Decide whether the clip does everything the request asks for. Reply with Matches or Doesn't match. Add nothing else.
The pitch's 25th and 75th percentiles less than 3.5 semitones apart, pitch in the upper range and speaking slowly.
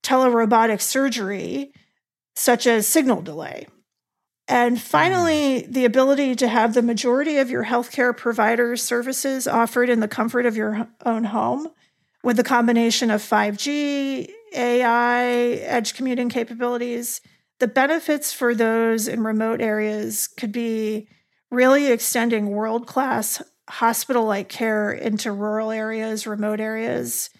Matches